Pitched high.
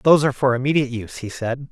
No: low, 130 Hz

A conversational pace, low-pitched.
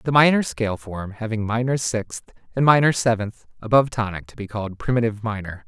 Yes: average, 180 wpm; low, 115 Hz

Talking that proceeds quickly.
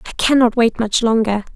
No: average, 190 wpm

